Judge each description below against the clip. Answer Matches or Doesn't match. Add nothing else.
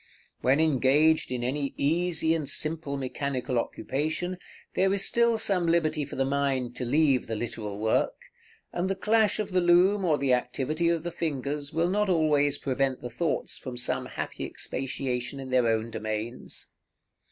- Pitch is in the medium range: Matches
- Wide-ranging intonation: Doesn't match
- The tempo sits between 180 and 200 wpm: Doesn't match